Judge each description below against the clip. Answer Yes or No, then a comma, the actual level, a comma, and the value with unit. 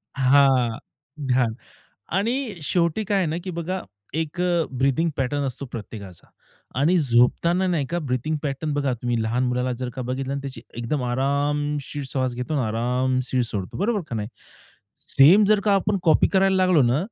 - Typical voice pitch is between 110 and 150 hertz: Yes, medium, 140 Hz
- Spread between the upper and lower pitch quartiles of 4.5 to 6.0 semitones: Yes, average, 5.2 semitones